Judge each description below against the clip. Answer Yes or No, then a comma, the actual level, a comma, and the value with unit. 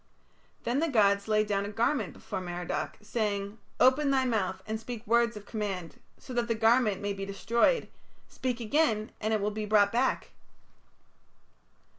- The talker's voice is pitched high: Yes, high, 215 Hz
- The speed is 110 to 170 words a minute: Yes, average, 165 wpm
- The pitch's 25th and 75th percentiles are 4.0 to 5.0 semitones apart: No, average, 2.9 semitones